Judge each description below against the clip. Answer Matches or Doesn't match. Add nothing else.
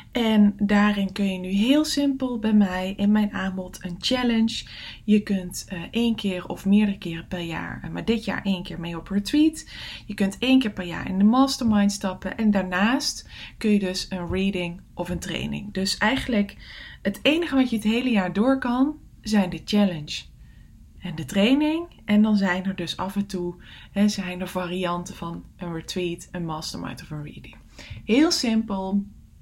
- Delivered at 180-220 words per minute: Matches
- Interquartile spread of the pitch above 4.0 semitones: Doesn't match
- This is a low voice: Doesn't match